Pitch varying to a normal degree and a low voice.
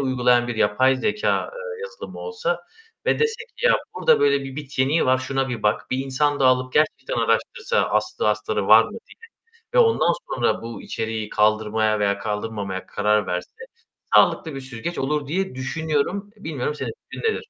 No: wide, 6.7 semitones; low, 130 Hz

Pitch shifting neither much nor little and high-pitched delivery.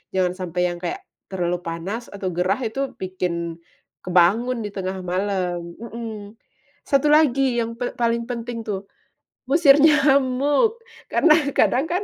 No: wide, 6.5 semitones; high, 225 Hz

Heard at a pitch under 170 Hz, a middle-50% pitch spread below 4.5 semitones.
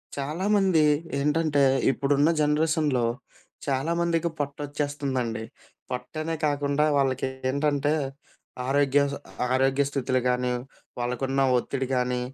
Yes: medium, 140 Hz; narrow, 2.4 semitones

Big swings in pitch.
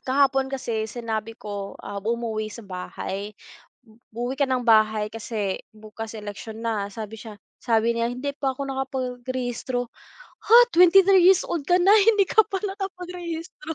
Yes: wide, 6.7 semitones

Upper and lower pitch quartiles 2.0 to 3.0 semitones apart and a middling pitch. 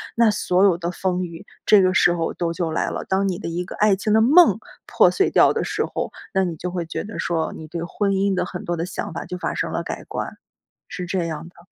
Yes: narrow, 2.5 semitones; medium, 180 Hz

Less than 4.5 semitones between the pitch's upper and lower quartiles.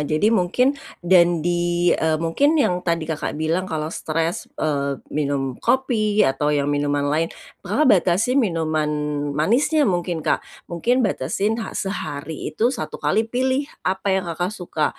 No: wide, 5.5 semitones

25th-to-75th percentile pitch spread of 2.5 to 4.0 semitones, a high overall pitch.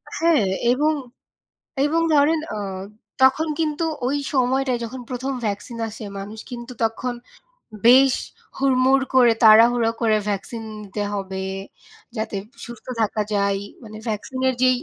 Yes: average, 3.6 semitones; high, 245 Hz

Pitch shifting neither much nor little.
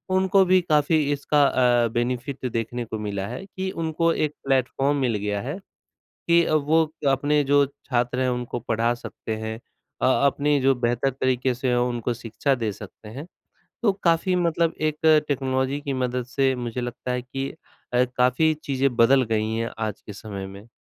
Yes: average, 3.4 semitones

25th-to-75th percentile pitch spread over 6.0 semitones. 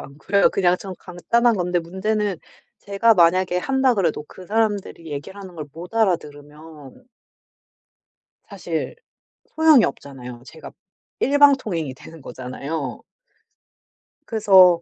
No: wide, 5.4 semitones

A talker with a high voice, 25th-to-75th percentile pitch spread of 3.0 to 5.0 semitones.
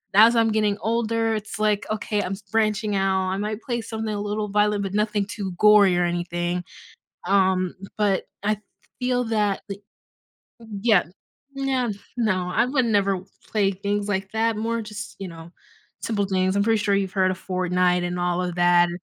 No: high, 205 Hz; narrow, 2.6 semitones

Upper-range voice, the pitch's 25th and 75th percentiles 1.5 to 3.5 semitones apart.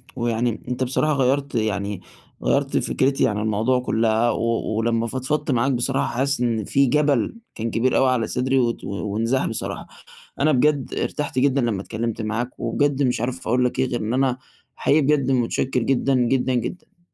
No: low, 125 Hz; average, 2.8 semitones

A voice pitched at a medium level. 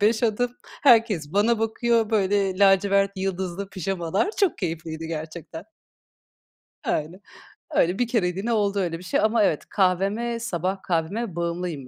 No: high, 195 Hz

